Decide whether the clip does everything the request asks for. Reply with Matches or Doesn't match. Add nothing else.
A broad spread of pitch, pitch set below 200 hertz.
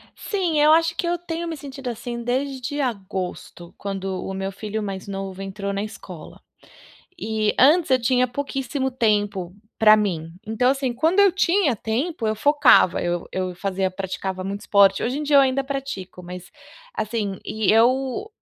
Doesn't match